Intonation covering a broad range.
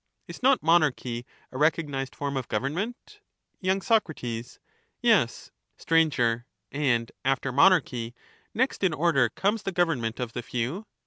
Yes: wide, 6.2 semitones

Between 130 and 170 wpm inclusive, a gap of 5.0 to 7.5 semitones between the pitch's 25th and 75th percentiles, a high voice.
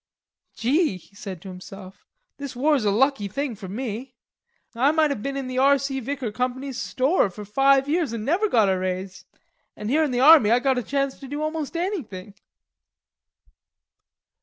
No: average, 180 wpm; average, 5.3 semitones; very high, 260 Hz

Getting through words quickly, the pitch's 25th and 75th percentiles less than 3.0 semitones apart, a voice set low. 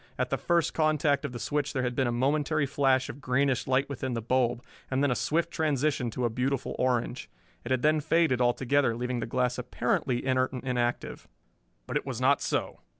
Yes: fast, 210 wpm; narrow, 2.6 semitones; low, 130 Hz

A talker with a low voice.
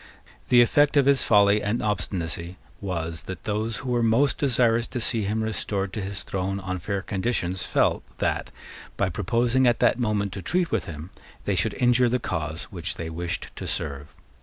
Yes: low, 105 Hz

